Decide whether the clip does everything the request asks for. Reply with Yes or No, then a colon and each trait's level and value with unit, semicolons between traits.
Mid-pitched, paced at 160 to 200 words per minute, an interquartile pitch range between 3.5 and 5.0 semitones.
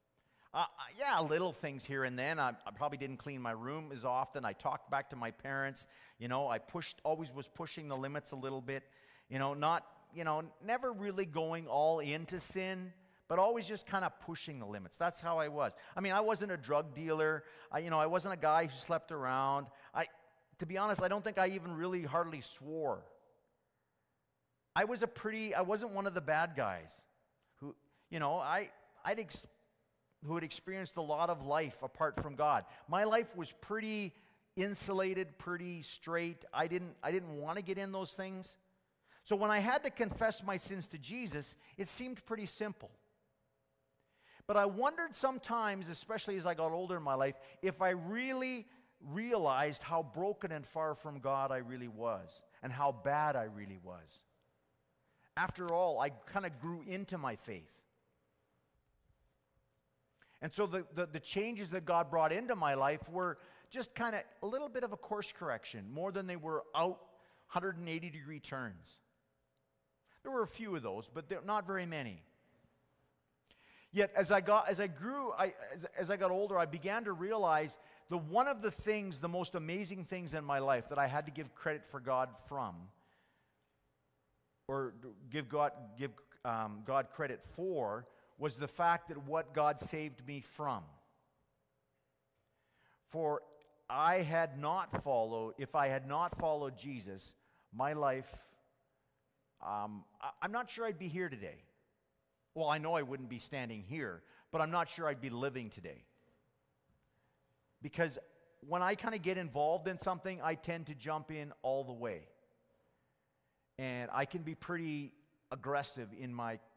No: medium, 160 Hz; average, 175 wpm; wide, 5.6 semitones